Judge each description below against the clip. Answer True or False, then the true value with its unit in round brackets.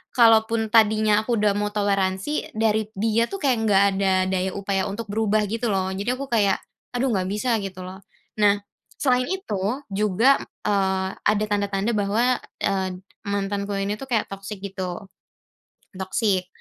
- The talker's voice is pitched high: True (205 Hz)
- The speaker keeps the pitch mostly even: True (2.3 semitones)